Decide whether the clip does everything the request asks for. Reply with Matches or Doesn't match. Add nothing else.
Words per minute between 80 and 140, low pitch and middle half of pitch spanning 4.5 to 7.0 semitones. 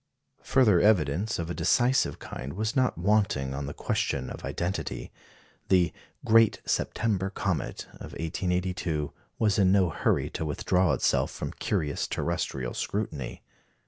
Matches